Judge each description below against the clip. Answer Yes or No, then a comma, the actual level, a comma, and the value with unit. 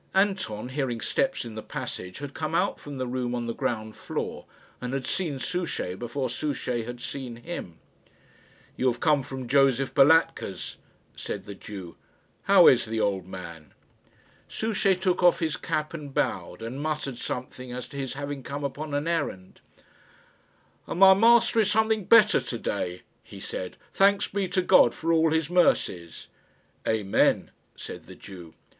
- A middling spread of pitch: No, wide, 6.3 semitones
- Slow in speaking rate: No, average, 165 wpm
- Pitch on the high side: No, low, 135 Hz